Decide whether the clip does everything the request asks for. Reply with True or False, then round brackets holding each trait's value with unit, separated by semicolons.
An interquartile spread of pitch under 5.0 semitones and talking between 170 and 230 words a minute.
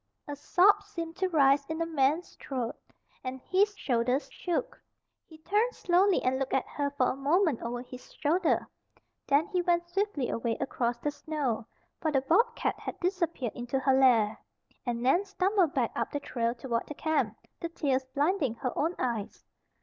False (5.5 semitones; 175 wpm)